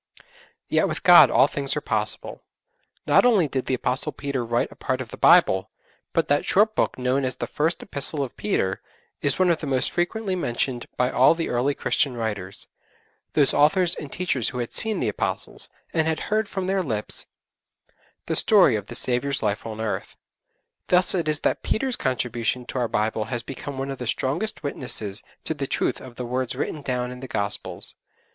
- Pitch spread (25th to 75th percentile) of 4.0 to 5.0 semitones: Yes, average, 4.7 semitones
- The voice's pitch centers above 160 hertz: No, low, 130 Hz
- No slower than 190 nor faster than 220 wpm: Yes, average, 195 wpm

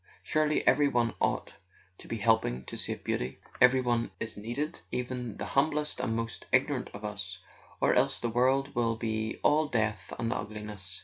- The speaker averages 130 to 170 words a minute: No, average, 180 wpm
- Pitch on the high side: No, low, 115 Hz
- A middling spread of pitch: Yes, average, 3.5 semitones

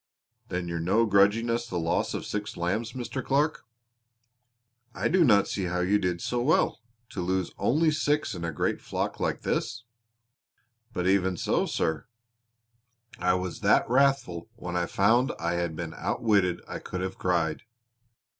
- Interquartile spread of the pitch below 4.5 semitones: No, average, 5.1 semitones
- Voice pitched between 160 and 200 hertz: No, very low, 95 Hz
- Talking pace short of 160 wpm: No, average, 165 wpm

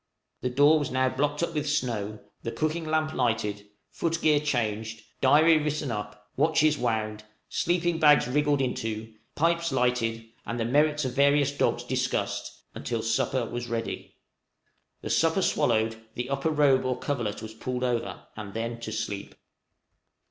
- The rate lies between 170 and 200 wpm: No, average, 155 wpm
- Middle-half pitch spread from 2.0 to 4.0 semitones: No, average, 4.9 semitones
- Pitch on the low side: Yes, low, 130 Hz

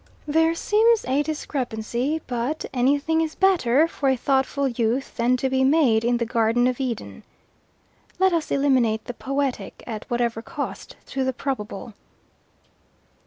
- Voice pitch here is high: Yes, very high, 265 Hz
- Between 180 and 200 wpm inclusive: No, average, 145 wpm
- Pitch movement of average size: Yes, average, 3.6 semitones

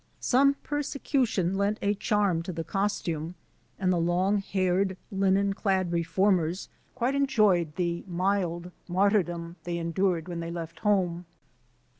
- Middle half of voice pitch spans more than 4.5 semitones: No, average, 2.8 semitones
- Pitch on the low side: No, medium, 185 Hz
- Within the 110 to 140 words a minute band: Yes, slow, 135 wpm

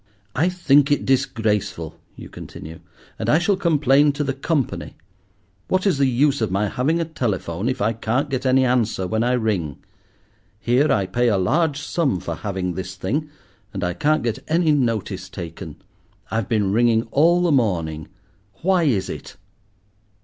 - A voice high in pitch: No, low, 120 Hz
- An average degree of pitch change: No, wide, 7.0 semitones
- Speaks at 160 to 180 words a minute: Yes, average, 170 wpm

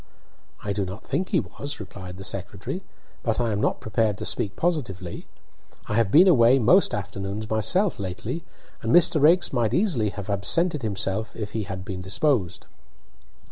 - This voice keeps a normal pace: Yes, average, 170 wpm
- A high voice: No, low, 110 Hz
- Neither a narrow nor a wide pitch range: No, wide, 6.6 semitones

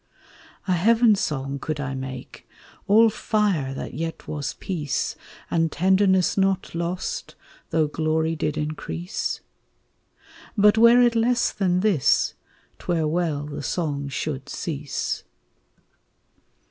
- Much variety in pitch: No, average, 4.9 semitones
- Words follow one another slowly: Yes, slow, 120 wpm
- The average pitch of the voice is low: No, medium, 165 Hz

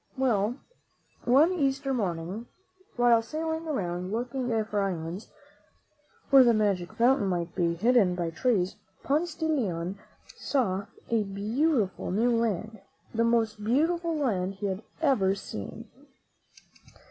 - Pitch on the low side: No, high, 225 Hz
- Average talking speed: No, slow, 125 wpm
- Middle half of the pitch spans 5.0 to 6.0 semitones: Yes, wide, 5.6 semitones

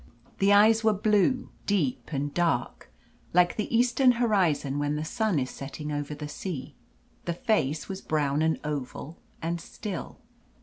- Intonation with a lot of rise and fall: Yes, wide, 6.2 semitones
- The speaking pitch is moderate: Yes, medium, 170 Hz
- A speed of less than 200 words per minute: Yes, average, 150 wpm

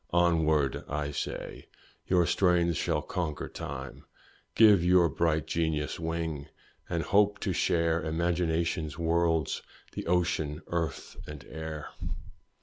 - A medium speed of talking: No, slow, 115 wpm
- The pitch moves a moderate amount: No, narrow, 1.9 semitones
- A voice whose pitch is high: No, very low, 80 Hz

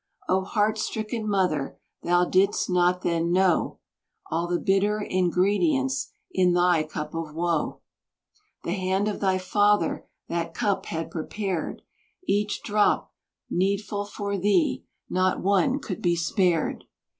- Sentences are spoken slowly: Yes, slow, 130 wpm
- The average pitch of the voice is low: No, medium, 185 Hz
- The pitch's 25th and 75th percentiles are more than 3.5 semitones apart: No, average, 2.9 semitones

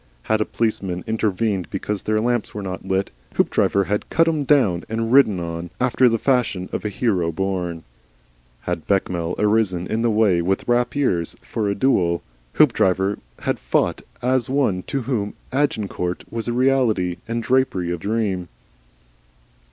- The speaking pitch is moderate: No, low, 105 Hz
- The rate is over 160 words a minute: No, average, 155 wpm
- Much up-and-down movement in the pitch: No, average, 4.7 semitones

